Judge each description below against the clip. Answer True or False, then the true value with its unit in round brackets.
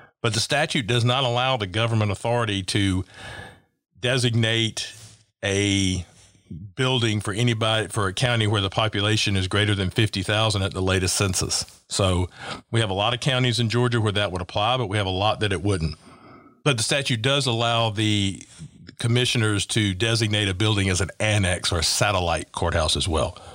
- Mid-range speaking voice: False (105 Hz)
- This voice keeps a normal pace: True (180 wpm)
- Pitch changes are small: False (3.3 semitones)